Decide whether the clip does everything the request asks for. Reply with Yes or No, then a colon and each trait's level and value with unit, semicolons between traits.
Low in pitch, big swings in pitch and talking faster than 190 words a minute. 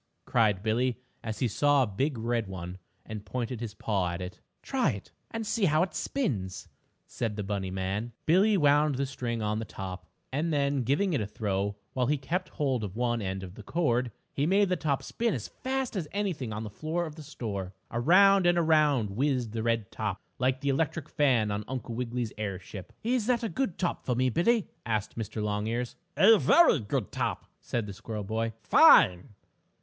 Yes: low, 125 Hz; wide, 6.7 semitones; average, 200 wpm